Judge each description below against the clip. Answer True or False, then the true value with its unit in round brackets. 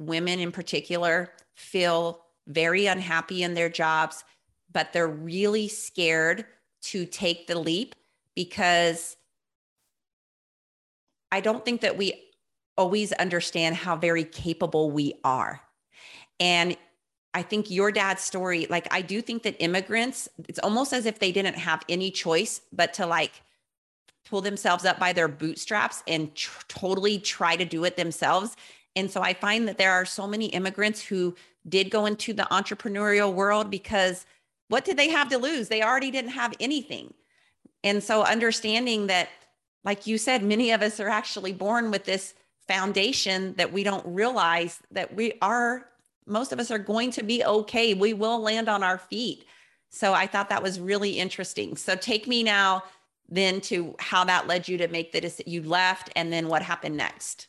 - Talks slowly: False (170 wpm)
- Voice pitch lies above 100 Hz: True (190 Hz)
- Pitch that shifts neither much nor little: True (3.6 semitones)